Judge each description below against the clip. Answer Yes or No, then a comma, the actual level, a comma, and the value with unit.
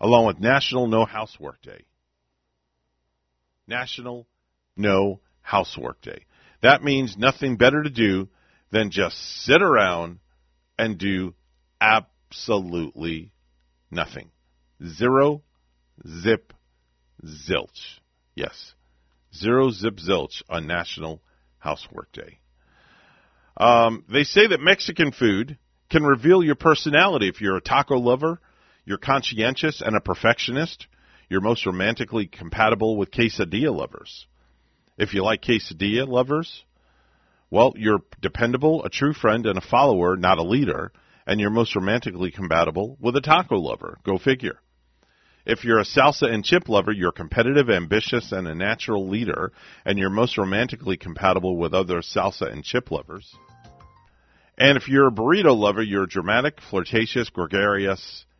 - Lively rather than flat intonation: Yes, wide, 6.8 semitones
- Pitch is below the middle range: Yes, low, 100 Hz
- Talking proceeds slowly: Yes, slow, 130 wpm